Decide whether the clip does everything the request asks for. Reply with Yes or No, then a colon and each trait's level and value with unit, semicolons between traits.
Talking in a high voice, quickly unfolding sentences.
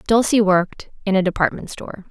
No: high, 195 Hz; average, 170 wpm